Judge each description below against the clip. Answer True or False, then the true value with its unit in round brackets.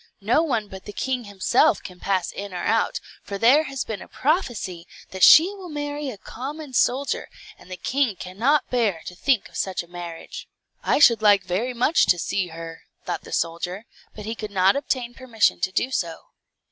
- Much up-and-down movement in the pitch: True (6.1 semitones)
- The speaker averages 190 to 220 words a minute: True (195 wpm)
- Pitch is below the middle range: False (215 Hz)